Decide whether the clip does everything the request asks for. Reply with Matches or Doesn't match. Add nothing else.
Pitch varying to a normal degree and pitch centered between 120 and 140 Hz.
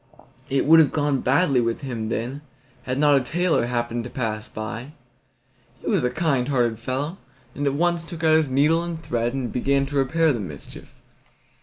Matches